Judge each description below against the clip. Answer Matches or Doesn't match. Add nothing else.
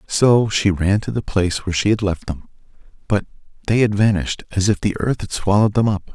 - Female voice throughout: Doesn't match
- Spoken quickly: Matches